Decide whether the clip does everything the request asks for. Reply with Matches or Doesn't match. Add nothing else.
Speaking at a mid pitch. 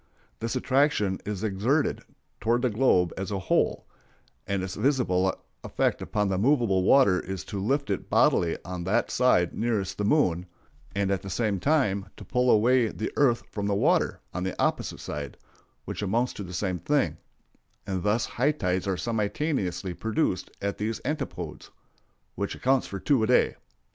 Doesn't match